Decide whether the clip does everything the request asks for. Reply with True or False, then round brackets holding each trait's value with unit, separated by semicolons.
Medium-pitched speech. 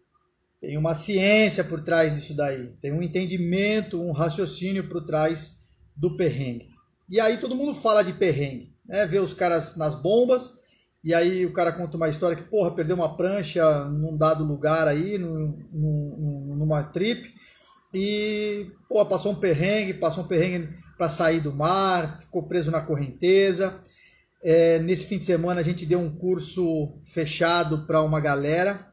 True (170 Hz)